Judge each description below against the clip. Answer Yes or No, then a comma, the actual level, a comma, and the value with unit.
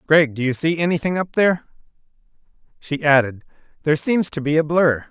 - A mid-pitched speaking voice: Yes, medium, 155 Hz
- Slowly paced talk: No, average, 175 wpm